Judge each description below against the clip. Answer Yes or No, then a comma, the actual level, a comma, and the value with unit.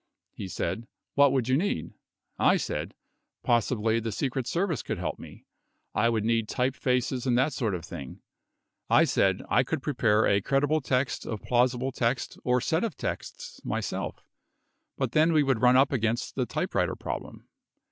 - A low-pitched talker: Yes, low, 125 Hz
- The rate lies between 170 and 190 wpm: Yes, average, 180 wpm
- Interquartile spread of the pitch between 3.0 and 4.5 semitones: Yes, average, 3.3 semitones